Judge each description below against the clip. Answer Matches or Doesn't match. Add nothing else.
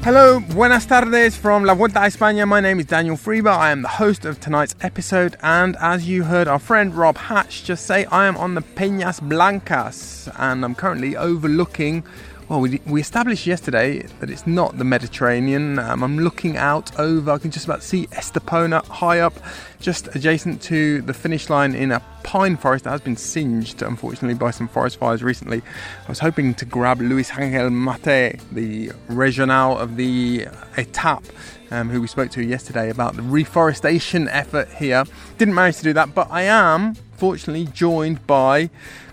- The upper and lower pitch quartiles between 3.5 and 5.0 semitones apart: Doesn't match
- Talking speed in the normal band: Matches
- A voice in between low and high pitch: Matches